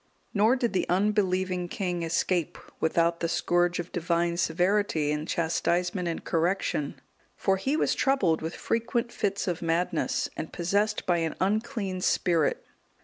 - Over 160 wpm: No, average, 145 wpm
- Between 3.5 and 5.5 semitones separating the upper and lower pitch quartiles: No, average, 3.1 semitones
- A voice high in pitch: No, medium, 180 Hz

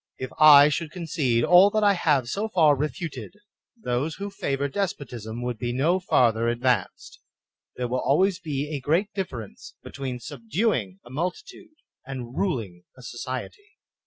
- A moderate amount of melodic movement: No, wide, 6.6 semitones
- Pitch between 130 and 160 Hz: Yes, medium, 140 Hz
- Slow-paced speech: No, average, 150 wpm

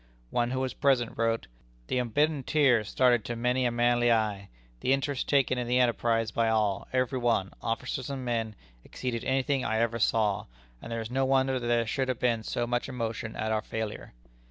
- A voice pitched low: Yes, low, 120 Hz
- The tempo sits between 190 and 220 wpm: Yes, fast, 205 wpm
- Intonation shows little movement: Yes, narrow, 2.3 semitones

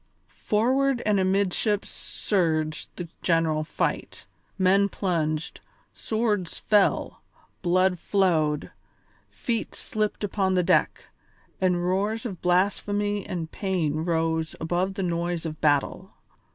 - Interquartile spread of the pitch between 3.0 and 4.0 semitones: Yes, average, 3.7 semitones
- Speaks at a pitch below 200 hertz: Yes, medium, 185 Hz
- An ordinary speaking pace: No, slow, 110 wpm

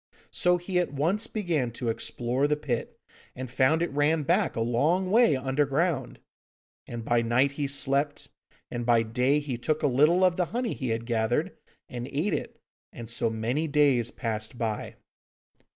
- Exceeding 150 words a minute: Yes, average, 170 wpm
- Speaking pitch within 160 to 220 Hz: No, low, 135 Hz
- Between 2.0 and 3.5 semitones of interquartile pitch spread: No, average, 4.7 semitones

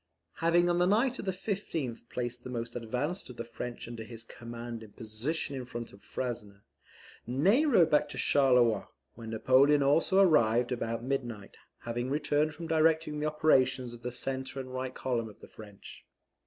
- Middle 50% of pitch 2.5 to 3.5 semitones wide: No, average, 4.6 semitones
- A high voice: No, low, 130 Hz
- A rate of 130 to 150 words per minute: No, average, 180 wpm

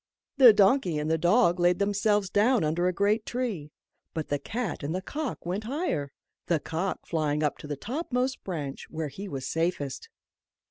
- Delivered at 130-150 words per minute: No, average, 180 wpm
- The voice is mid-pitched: Yes, medium, 180 Hz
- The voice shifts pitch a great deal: Yes, wide, 5.9 semitones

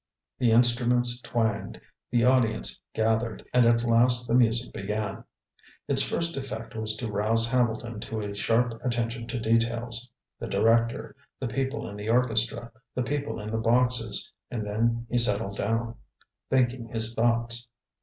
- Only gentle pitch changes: Yes, narrow, 1.6 semitones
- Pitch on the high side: No, low, 115 Hz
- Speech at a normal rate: Yes, average, 150 wpm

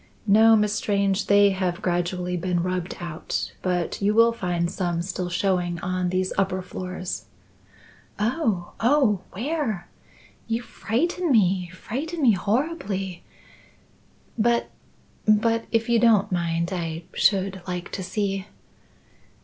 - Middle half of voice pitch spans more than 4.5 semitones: No, average, 3.8 semitones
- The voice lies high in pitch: Yes, high, 195 Hz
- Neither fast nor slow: No, slow, 125 wpm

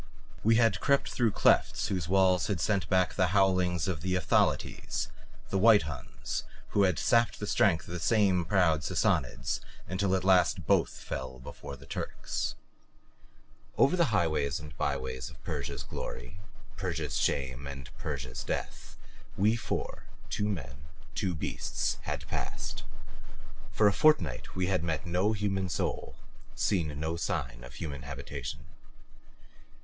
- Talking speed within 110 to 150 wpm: Yes, average, 145 wpm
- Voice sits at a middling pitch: No, very low, 90 Hz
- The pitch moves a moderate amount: No, wide, 5.7 semitones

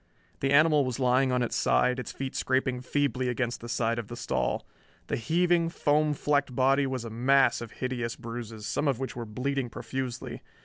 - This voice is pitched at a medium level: No, low, 130 Hz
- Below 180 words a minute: No, average, 190 wpm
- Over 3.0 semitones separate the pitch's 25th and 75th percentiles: No, average, 2.7 semitones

